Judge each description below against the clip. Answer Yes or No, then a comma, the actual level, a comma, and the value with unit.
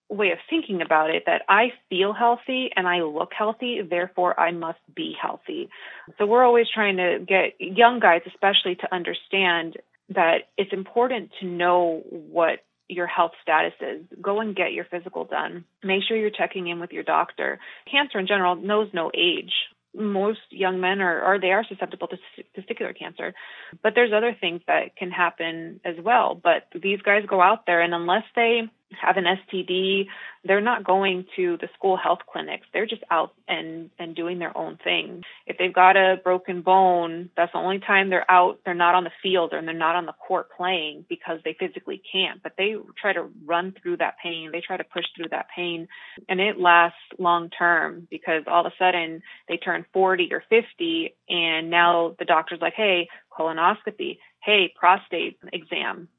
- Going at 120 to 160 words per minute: No, average, 190 wpm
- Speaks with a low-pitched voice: No, medium, 185 Hz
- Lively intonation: No, average, 3.3 semitones